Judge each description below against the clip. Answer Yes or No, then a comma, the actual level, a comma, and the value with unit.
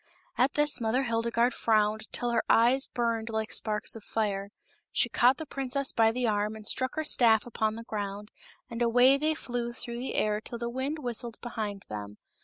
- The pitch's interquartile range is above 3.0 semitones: No, narrow, 2.5 semitones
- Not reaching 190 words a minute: No, average, 195 wpm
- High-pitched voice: Yes, high, 235 Hz